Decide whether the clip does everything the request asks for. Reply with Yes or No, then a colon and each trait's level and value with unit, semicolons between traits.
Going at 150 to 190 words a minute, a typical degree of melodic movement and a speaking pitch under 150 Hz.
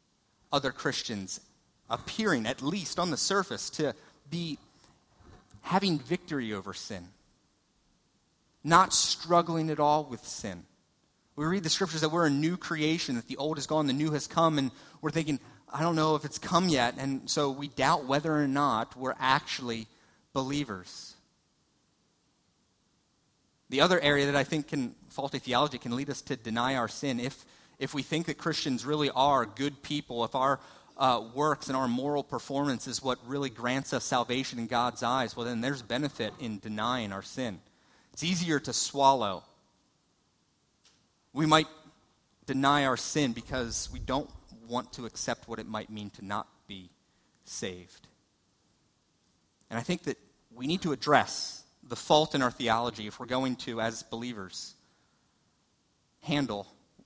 Yes: average, 160 wpm; average, 4.2 semitones; low, 135 Hz